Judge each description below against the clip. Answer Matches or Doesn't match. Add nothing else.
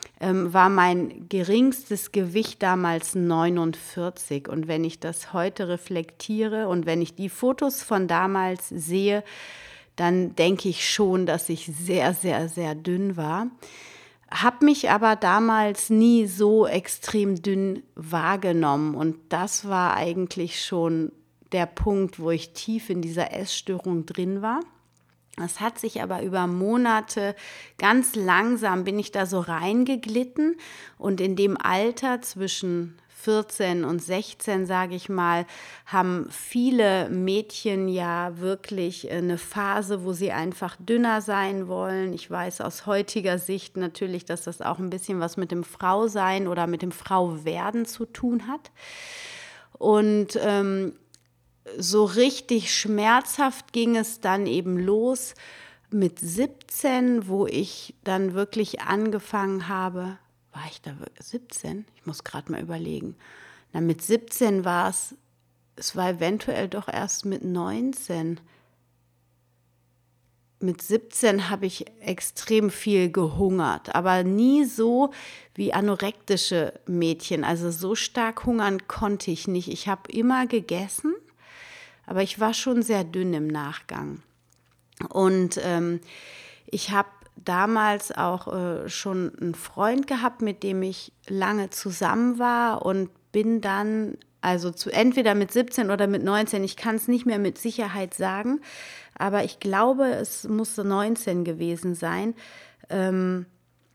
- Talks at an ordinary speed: Matches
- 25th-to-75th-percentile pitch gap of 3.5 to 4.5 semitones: Matches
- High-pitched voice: Matches